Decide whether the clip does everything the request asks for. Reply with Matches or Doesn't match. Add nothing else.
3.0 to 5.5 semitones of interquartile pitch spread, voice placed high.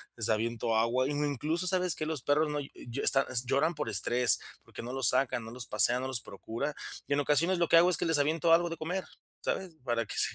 Doesn't match